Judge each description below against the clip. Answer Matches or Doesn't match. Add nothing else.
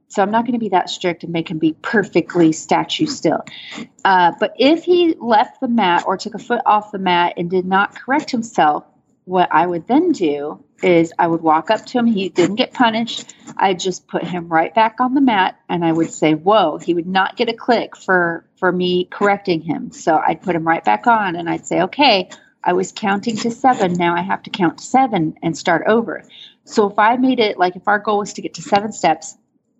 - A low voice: Doesn't match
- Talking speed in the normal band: Doesn't match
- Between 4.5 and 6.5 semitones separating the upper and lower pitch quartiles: Matches